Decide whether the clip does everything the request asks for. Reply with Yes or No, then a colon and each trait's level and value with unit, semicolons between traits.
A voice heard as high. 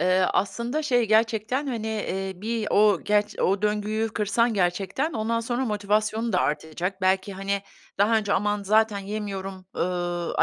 Yes: high, 210 Hz